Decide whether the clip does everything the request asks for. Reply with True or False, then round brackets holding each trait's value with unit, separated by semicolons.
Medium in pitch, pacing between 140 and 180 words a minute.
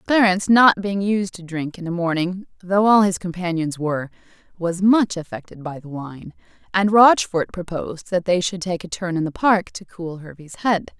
False (180 Hz; 195 wpm)